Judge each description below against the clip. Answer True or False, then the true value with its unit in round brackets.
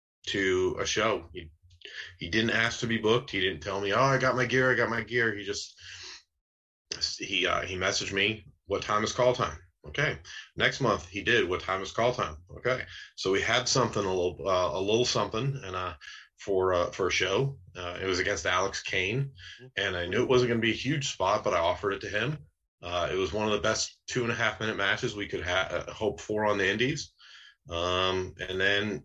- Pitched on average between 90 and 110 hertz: True (105 Hz)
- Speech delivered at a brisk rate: True (225 wpm)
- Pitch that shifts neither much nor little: True (5.0 semitones)